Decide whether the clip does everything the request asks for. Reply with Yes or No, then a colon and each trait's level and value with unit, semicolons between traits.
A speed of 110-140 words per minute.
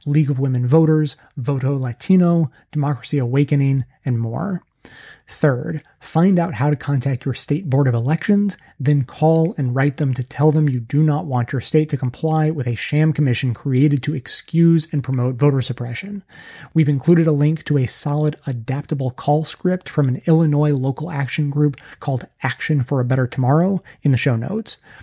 No: average, 175 wpm